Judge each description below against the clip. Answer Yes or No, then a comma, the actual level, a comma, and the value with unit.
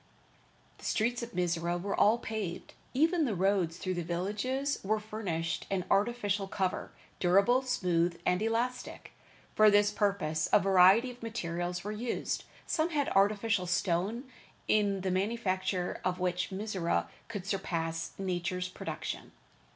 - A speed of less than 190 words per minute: Yes, slow, 135 wpm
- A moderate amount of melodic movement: Yes, average, 3.7 semitones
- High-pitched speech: Yes, high, 195 Hz